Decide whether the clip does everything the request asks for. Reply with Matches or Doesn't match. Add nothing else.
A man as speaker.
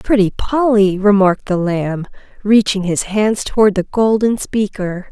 Doesn't match